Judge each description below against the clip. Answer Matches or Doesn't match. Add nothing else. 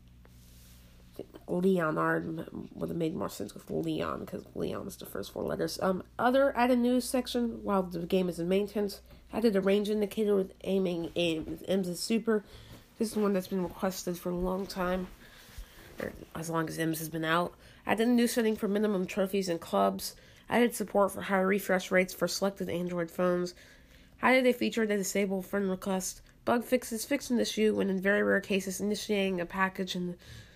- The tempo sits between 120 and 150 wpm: Doesn't match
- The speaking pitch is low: Doesn't match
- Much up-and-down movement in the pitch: Doesn't match